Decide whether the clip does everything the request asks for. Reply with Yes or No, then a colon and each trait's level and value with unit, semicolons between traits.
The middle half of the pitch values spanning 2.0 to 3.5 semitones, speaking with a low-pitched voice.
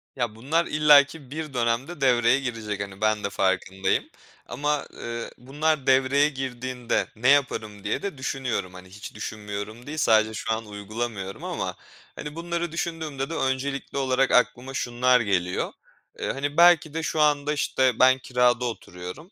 No: average, 4.7 semitones; low, 130 Hz